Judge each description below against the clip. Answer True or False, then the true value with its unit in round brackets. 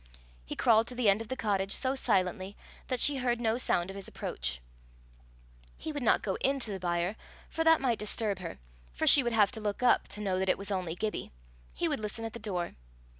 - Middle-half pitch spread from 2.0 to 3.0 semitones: False (4.1 semitones)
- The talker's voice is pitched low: False (210 Hz)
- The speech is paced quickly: True (225 wpm)